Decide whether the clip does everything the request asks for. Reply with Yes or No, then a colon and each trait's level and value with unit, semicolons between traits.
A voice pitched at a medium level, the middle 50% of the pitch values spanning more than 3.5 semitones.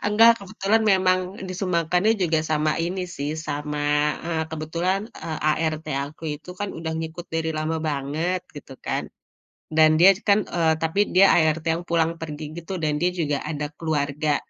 No: medium, 160 Hz; average, 2.8 semitones